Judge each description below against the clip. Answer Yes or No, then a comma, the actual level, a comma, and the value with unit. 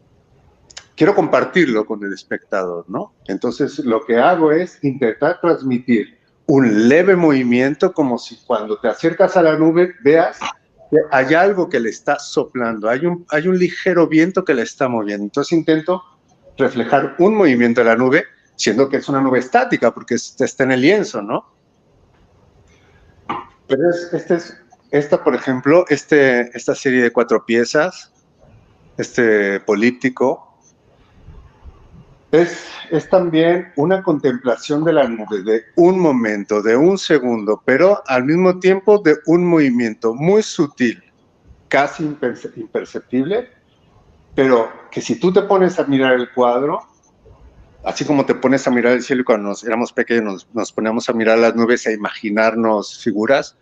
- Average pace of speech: Yes, average, 150 wpm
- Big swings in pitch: Yes, wide, 6.0 semitones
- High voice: No, low, 135 Hz